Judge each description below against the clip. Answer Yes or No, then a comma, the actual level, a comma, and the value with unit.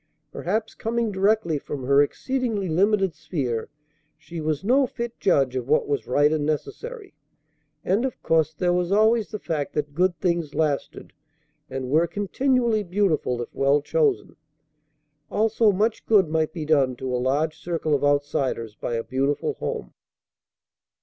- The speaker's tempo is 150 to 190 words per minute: Yes, average, 155 wpm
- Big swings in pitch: Yes, wide, 6.7 semitones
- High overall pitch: No, medium, 160 Hz